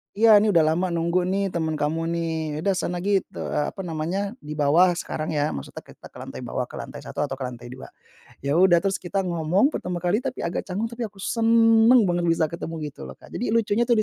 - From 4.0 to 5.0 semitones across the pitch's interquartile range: Yes, average, 4.4 semitones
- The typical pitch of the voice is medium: Yes, medium, 175 Hz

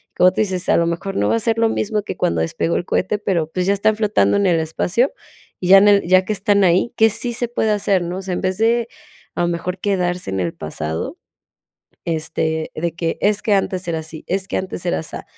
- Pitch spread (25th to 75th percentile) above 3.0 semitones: Yes, average, 3.5 semitones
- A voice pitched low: No, medium, 185 Hz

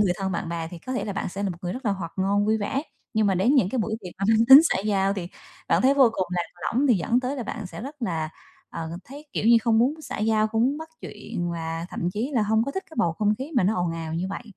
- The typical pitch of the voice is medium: No, high, 210 Hz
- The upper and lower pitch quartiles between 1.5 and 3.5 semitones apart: No, wide, 5.5 semitones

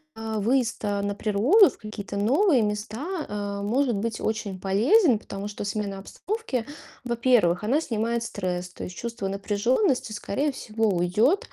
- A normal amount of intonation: Yes, average, 3.8 semitones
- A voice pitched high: Yes, high, 220 Hz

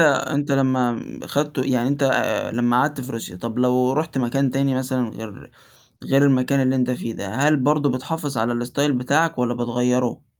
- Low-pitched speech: Yes, low, 130 Hz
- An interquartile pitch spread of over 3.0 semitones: No, narrow, 2.4 semitones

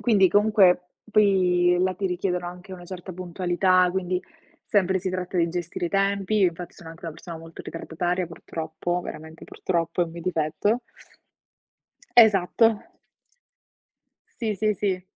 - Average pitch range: No, narrow, 2.0 semitones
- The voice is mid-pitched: Yes, medium, 180 Hz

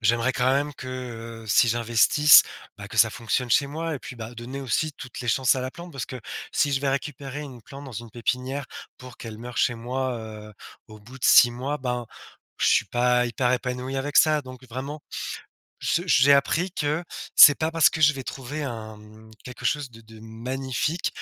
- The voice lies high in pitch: No, low, 130 Hz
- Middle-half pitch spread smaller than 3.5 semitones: Yes, average, 3.0 semitones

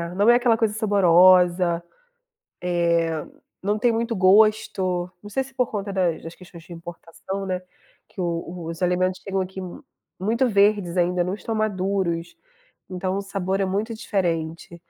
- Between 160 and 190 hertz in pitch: Yes, medium, 185 Hz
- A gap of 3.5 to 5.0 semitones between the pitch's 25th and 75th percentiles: No, average, 2.9 semitones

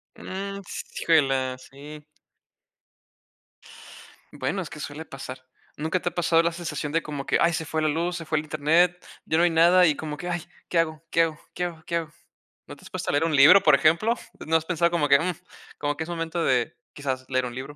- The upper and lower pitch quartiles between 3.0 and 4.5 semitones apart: No, narrow, 2.6 semitones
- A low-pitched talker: No, medium, 160 Hz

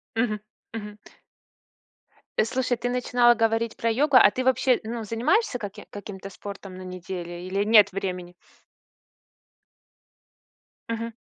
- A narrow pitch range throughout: No, average, 3.5 semitones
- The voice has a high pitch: Yes, high, 220 Hz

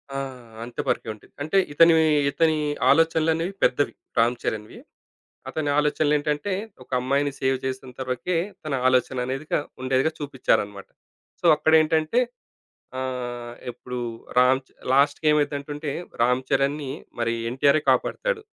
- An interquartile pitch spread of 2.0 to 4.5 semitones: Yes, average, 3.4 semitones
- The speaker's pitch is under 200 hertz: Yes, medium, 140 Hz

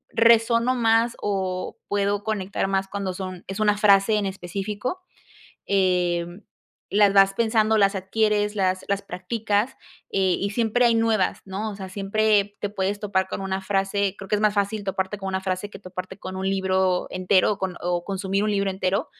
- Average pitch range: No, narrow, 1.8 semitones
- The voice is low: No, high, 200 Hz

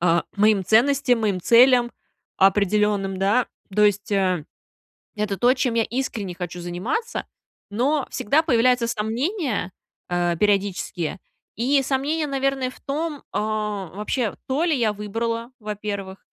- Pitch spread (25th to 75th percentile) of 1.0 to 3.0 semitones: No, average, 4.7 semitones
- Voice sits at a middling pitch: No, high, 215 Hz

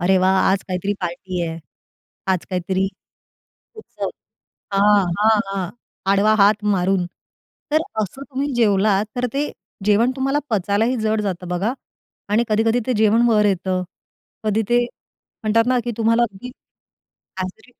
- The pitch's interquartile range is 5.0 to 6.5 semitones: No, average, 3.4 semitones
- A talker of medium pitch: No, high, 210 Hz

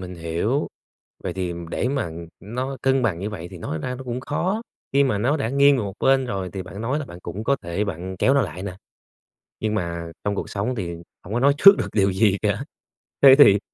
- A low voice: Yes, low, 105 Hz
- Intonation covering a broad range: Yes, wide, 6.5 semitones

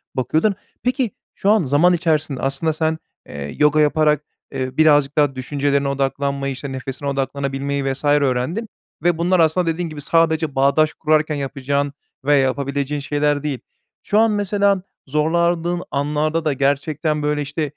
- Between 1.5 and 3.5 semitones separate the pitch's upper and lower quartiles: Yes, narrow, 2.6 semitones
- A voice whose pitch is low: No, medium, 150 Hz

